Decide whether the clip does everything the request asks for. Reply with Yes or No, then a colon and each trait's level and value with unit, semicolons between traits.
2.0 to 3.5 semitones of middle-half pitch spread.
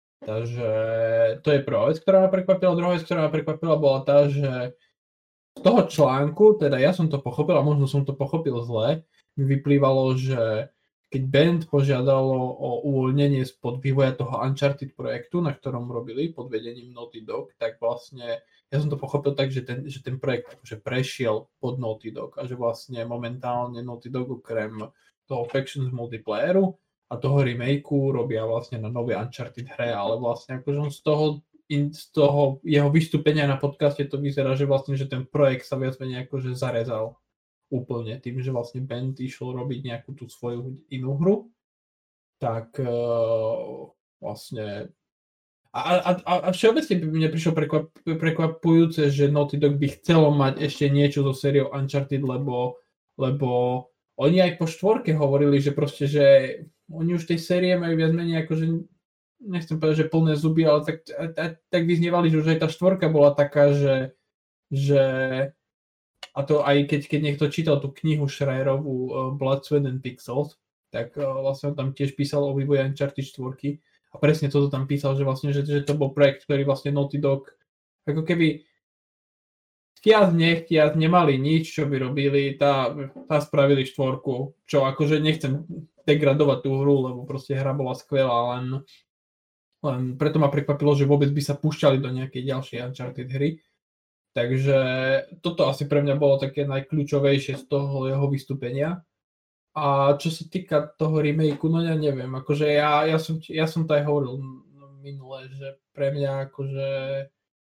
Yes: narrow, 2.5 semitones